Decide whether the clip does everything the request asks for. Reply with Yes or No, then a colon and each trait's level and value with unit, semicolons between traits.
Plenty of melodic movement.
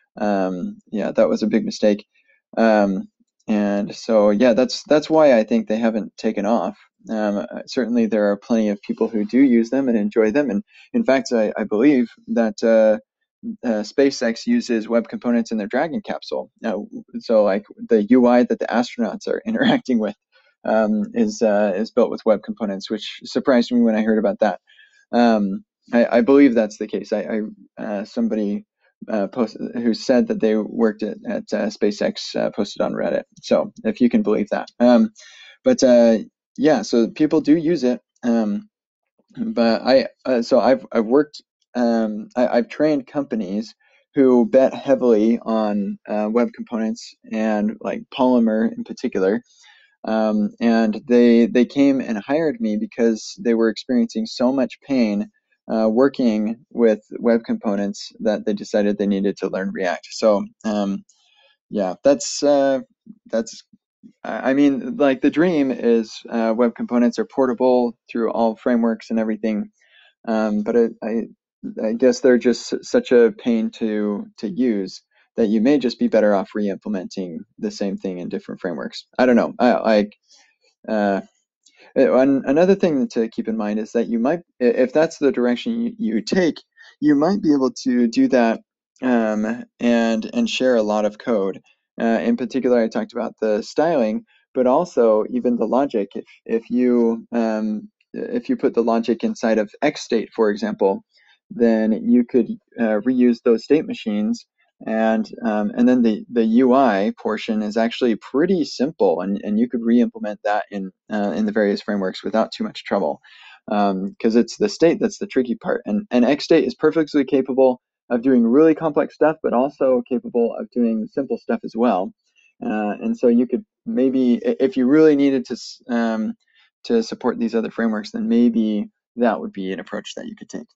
Yes: wide, 8.1 semitones